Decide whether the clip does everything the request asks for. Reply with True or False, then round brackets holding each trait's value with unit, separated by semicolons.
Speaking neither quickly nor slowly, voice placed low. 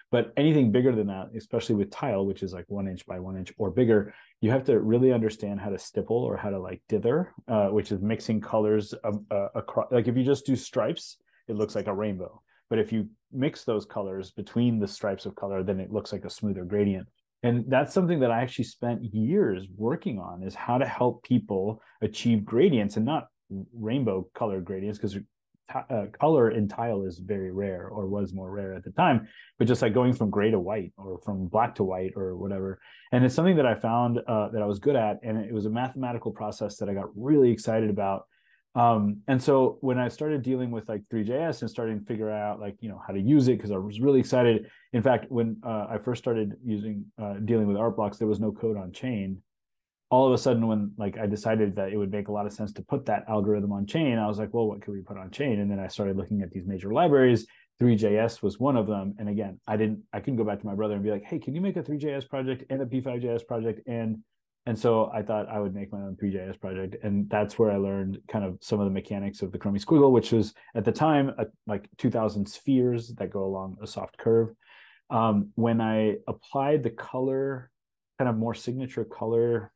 False (240 wpm; 110 Hz)